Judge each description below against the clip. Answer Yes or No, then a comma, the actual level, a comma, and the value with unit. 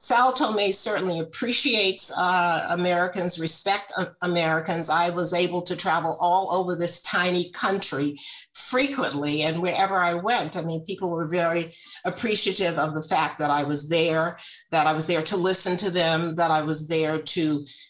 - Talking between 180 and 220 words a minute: No, average, 170 wpm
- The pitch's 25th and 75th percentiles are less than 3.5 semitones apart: Yes, narrow, 2.6 semitones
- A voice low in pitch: No, medium, 175 Hz